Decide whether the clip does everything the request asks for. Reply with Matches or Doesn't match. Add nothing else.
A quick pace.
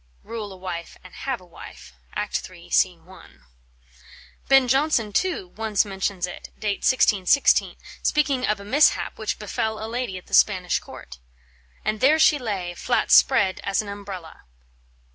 Doesn't match